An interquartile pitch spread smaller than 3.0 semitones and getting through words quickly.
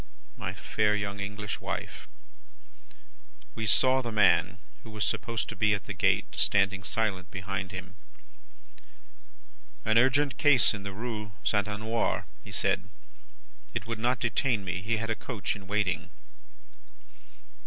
No: narrow, 2.6 semitones; average, 145 wpm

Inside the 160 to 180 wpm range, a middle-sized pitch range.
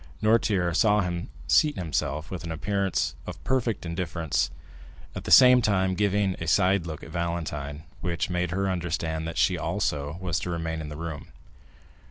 Yes: average, 170 wpm; average, 3.2 semitones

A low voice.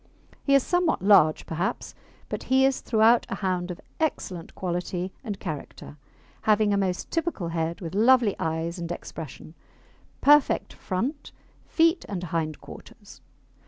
No: high, 190 Hz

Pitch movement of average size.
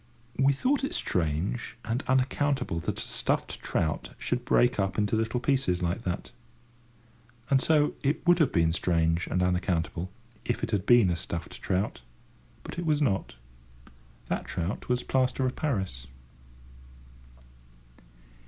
No: wide, 7.1 semitones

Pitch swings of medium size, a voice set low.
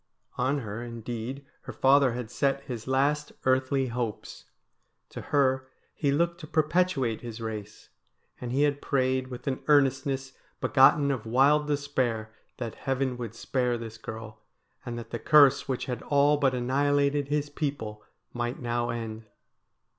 Yes: average, 3.1 semitones; low, 130 Hz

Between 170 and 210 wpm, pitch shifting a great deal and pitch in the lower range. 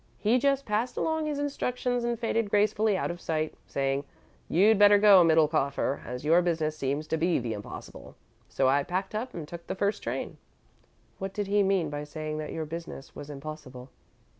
No: average, 190 wpm; wide, 5.8 semitones; medium, 170 Hz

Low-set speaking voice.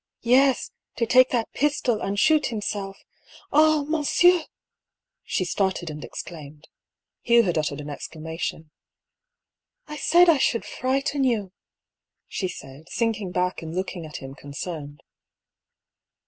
No: high, 200 Hz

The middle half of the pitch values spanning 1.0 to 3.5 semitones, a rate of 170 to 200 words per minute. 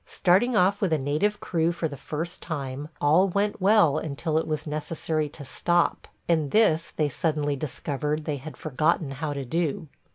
Yes: average, 2.9 semitones; average, 175 wpm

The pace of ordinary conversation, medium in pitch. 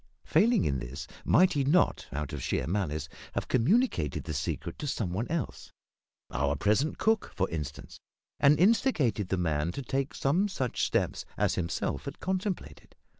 No: average, 165 wpm; low, 120 Hz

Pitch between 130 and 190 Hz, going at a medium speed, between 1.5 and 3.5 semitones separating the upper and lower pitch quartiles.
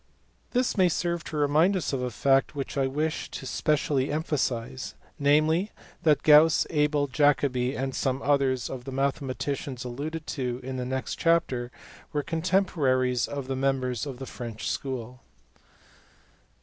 Yes: medium, 140 Hz; average, 150 wpm; average, 2.9 semitones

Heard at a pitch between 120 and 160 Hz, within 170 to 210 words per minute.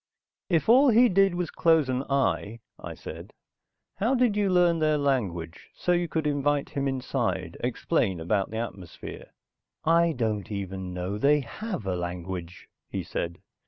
No: medium, 140 Hz; average, 160 wpm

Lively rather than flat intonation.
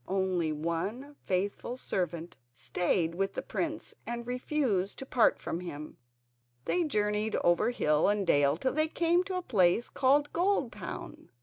Yes: wide, 7.2 semitones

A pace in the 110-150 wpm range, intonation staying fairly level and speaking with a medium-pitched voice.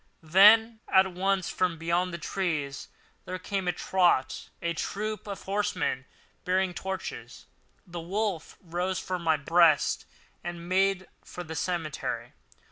Yes: average, 140 wpm; narrow, 2.3 semitones; medium, 180 Hz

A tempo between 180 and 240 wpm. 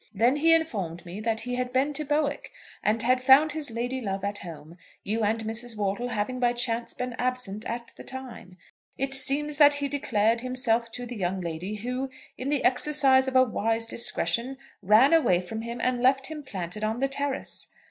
Yes: average, 200 wpm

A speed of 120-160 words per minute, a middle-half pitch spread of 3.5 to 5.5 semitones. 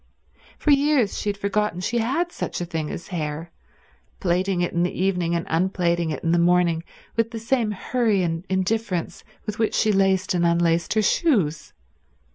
No: average, 180 wpm; average, 4.1 semitones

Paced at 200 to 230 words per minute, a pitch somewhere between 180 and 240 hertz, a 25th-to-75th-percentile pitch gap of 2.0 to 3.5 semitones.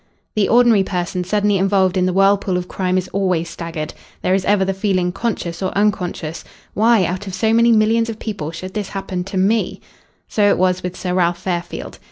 Yes: fast, 205 wpm; high, 190 Hz; narrow, 2.4 semitones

